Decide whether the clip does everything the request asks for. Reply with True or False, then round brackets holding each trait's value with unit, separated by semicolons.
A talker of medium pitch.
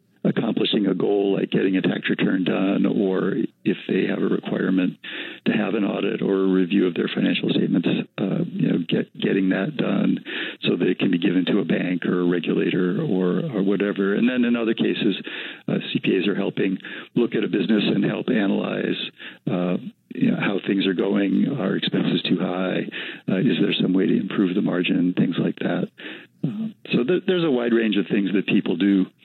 False (95 Hz)